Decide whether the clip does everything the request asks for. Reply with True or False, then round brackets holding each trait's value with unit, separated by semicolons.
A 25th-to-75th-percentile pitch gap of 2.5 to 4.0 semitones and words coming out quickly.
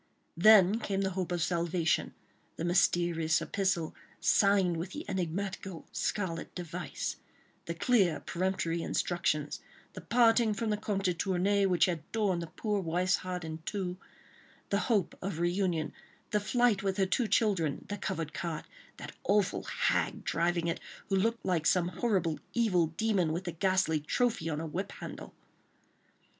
False (3.2 semitones; 155 wpm)